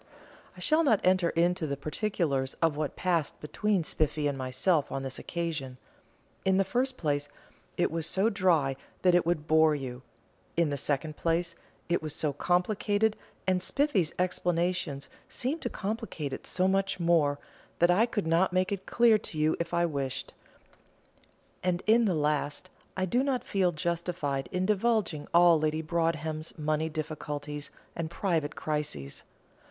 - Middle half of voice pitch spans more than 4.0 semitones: No, average, 3.7 semitones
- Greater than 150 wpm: Yes, average, 160 wpm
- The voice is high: No, medium, 170 Hz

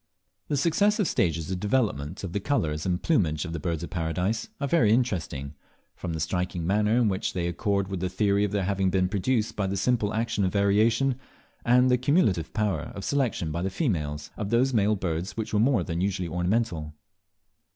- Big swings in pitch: No, average, 4.8 semitones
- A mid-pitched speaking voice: No, low, 100 Hz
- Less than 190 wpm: No, average, 200 wpm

